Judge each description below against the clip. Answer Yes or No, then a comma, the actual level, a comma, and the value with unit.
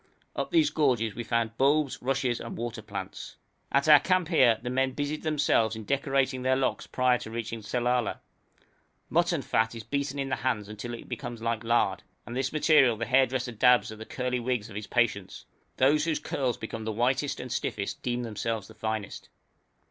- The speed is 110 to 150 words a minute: No, average, 190 wpm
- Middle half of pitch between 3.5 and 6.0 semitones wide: No, average, 3.1 semitones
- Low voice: Yes, low, 125 Hz